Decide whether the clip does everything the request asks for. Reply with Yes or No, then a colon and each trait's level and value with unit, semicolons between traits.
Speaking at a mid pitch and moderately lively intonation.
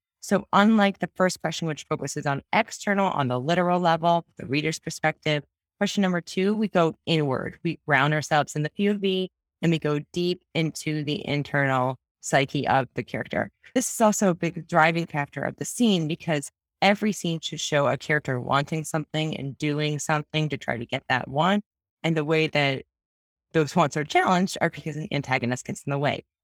Yes: medium, 155 Hz; average, 3.6 semitones